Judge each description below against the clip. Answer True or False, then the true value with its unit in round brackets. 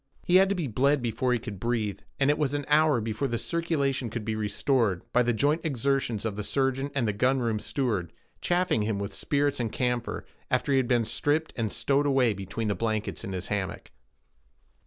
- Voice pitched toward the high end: False (125 Hz)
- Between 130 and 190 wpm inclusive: False (205 wpm)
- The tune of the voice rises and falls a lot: False (4.4 semitones)